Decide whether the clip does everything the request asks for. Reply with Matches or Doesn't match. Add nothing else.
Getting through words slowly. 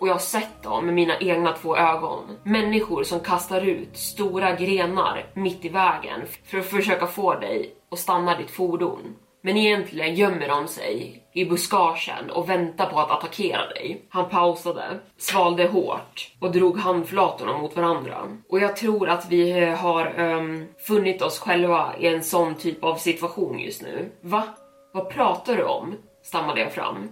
Doesn't match